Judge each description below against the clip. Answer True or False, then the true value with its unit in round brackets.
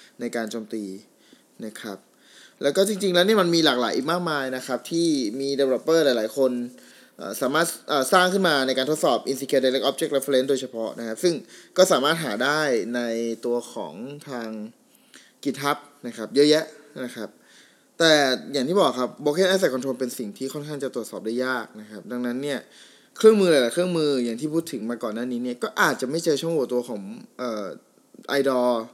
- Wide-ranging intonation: False (4.2 semitones)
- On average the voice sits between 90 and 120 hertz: False (135 Hz)